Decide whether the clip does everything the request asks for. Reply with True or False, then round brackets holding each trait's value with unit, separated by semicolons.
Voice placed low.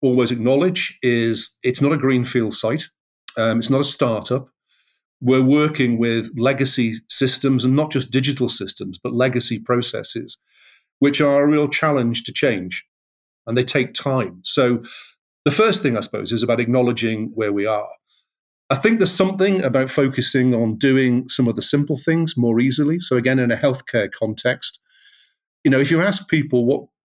True (130 Hz)